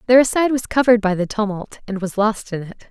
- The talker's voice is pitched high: Yes, high, 215 Hz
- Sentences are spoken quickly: Yes, fast, 250 wpm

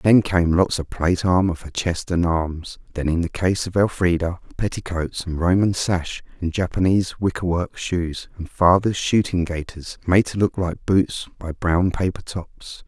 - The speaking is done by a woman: No, male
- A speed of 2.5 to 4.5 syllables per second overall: Yes, 4.4 syllables/s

